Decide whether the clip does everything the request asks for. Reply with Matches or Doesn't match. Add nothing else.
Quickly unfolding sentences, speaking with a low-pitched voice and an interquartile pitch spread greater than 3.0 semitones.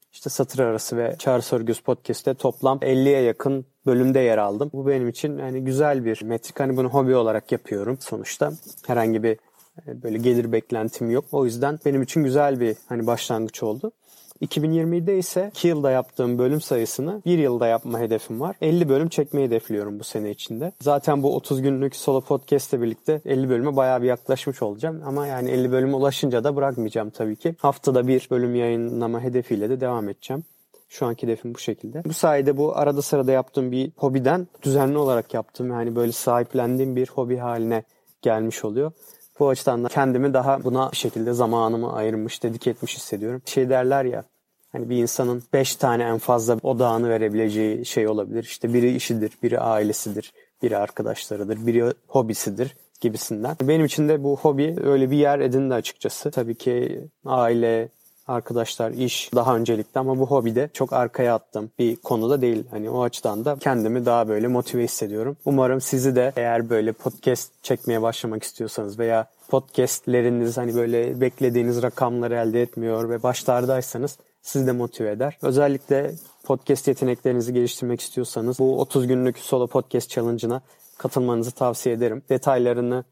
Doesn't match